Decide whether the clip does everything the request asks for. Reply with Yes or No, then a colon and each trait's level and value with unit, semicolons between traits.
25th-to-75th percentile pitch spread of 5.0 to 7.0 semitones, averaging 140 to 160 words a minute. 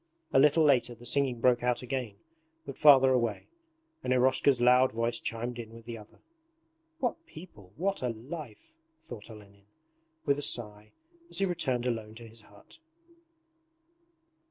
No: average, 3.3 semitones; average, 155 wpm